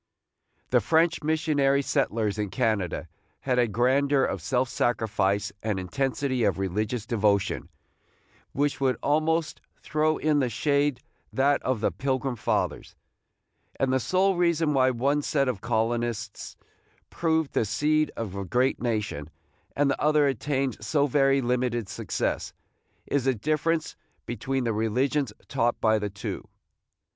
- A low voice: Yes, low, 130 Hz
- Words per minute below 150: Yes, average, 140 wpm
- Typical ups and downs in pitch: Yes, average, 4.6 semitones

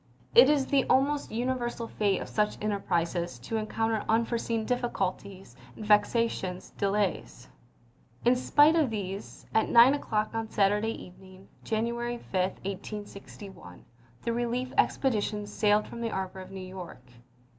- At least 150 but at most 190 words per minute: No, average, 140 wpm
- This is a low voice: No, high, 215 Hz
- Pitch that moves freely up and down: No, average, 3.6 semitones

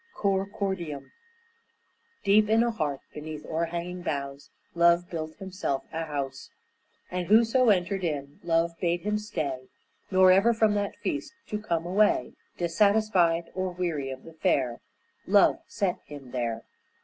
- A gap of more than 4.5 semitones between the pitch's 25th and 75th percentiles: Yes, average, 4.9 semitones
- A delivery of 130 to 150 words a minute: Yes, average, 145 wpm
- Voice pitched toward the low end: No, medium, 175 Hz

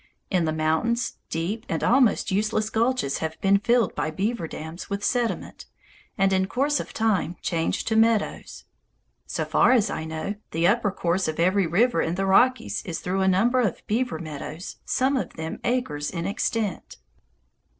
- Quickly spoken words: No, average, 170 wpm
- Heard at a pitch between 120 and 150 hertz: No, high, 195 Hz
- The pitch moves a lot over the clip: Yes, wide, 5.7 semitones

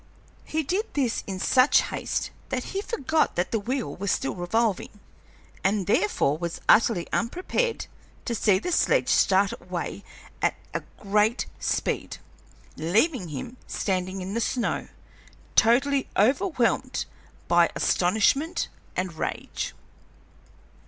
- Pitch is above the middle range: Yes, high, 220 Hz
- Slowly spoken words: Yes, slow, 120 wpm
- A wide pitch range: Yes, wide, 6.4 semitones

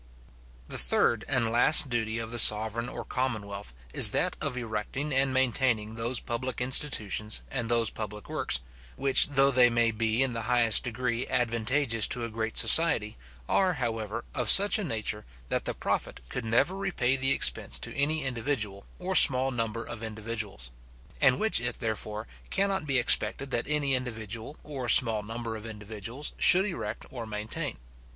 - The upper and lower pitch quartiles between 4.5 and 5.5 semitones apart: No, average, 3.3 semitones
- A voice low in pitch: Yes, low, 120 Hz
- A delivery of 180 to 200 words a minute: No, average, 165 wpm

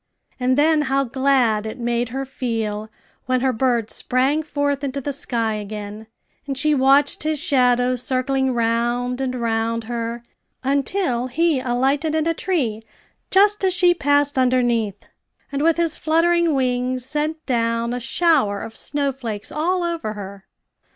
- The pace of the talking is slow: No, average, 150 wpm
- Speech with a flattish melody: No, average, 3.9 semitones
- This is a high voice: Yes, very high, 255 Hz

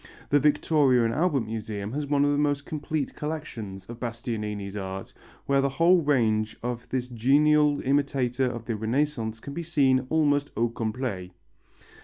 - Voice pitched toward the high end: No, low, 130 Hz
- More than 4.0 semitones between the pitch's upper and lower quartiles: Yes, average, 4.4 semitones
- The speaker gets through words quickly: No, average, 160 wpm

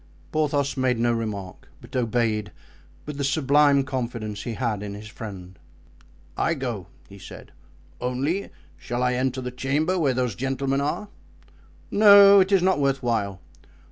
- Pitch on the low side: Yes, low, 130 Hz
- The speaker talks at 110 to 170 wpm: Yes, average, 150 wpm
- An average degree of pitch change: Yes, average, 4.0 semitones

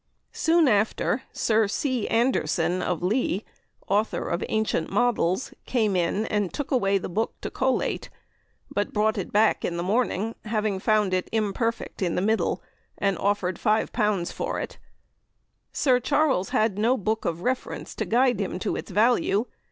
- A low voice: No, high, 215 Hz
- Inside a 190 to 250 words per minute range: No, average, 160 wpm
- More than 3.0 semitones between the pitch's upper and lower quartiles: Yes, average, 3.5 semitones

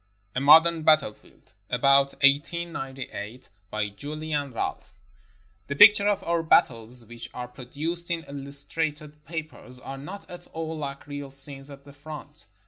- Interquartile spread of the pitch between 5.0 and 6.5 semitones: No, average, 3.1 semitones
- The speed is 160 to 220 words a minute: No, average, 140 wpm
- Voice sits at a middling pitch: Yes, medium, 145 Hz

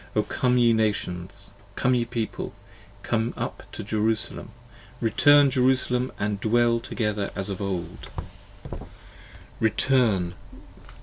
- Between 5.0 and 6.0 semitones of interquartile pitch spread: No, average, 3.6 semitones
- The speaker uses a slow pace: Yes, slow, 115 wpm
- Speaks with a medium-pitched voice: No, low, 110 Hz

